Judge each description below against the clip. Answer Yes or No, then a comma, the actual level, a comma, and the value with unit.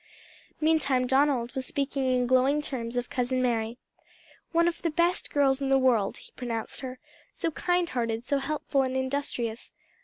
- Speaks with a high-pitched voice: Yes, very high, 260 Hz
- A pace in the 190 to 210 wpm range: No, average, 165 wpm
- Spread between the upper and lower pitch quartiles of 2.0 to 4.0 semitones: Yes, average, 2.7 semitones